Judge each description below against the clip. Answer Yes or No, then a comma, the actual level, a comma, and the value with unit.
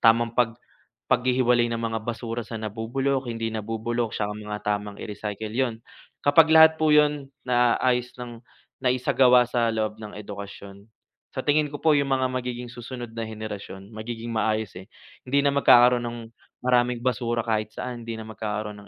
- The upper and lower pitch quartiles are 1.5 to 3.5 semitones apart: Yes, narrow, 2.4 semitones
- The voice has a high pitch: No, low, 120 Hz